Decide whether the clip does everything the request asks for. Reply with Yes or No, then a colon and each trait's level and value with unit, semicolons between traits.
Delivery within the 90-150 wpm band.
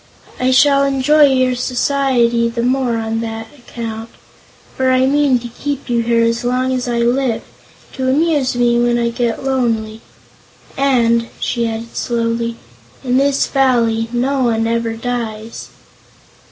Yes: average, 145 wpm